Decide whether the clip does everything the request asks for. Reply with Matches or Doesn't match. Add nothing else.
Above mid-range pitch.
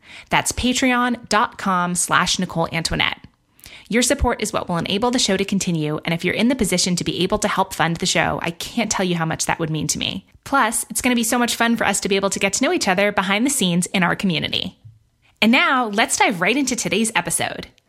Matches